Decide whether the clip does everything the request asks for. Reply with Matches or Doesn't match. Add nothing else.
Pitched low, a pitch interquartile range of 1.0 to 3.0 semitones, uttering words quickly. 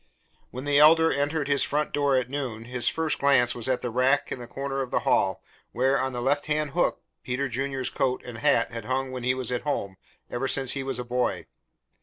Matches